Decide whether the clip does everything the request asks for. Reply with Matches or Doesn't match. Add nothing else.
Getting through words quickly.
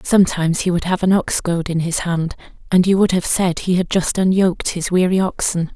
Matches